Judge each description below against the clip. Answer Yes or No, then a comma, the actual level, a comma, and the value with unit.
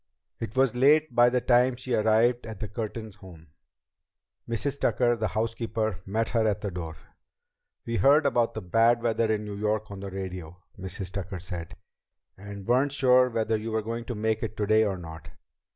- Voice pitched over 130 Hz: No, low, 110 Hz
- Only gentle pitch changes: No, average, 3.2 semitones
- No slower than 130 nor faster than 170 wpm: No, average, 185 wpm